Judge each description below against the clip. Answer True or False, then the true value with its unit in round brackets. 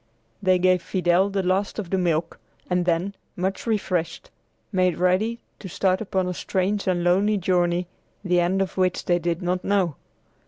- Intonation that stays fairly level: True (1.6 semitones)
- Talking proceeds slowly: False (170 wpm)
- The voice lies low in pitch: False (185 Hz)